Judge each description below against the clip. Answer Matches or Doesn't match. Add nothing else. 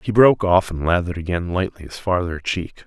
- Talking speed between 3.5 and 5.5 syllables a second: Doesn't match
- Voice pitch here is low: Matches